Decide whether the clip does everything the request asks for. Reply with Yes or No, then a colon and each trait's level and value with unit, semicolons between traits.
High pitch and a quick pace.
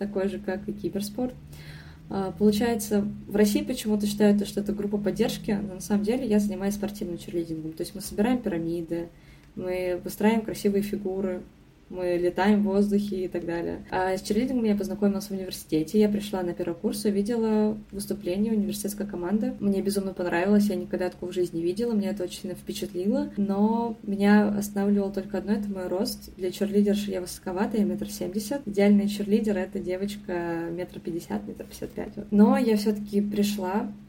Yes: high, 200 Hz; fast, 170 wpm